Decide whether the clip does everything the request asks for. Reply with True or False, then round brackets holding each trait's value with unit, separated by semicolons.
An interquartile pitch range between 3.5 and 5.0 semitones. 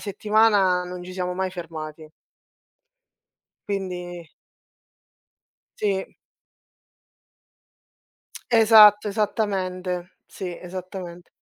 False (2.4 semitones)